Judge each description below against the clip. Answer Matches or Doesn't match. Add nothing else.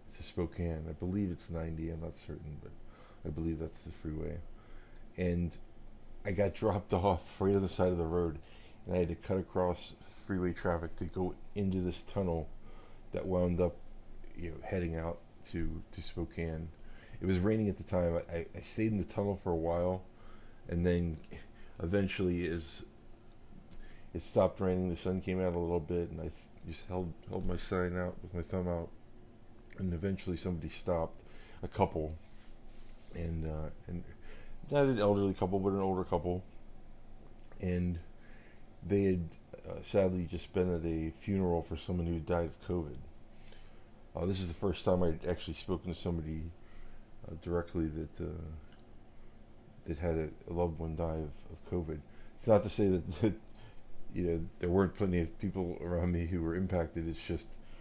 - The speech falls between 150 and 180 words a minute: Matches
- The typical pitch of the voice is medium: Doesn't match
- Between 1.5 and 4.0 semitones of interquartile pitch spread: Matches